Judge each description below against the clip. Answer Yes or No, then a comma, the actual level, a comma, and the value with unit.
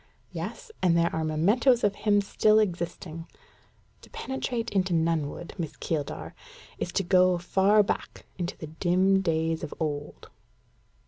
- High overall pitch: No, medium, 180 Hz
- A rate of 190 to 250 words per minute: No, average, 140 wpm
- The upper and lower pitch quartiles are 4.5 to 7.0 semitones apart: No, average, 3.9 semitones